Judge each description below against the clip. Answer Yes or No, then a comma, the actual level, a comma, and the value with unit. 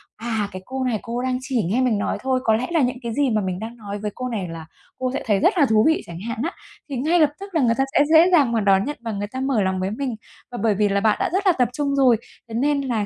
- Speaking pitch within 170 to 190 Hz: No, high, 240 Hz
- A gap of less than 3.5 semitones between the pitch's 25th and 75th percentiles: No, average, 4.2 semitones